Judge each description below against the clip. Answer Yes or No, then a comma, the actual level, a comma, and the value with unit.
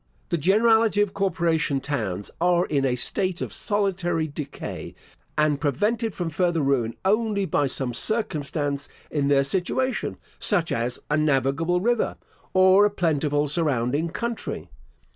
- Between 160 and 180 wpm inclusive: No, slow, 135 wpm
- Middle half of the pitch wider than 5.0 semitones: Yes, wide, 5.6 semitones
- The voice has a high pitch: No, medium, 165 Hz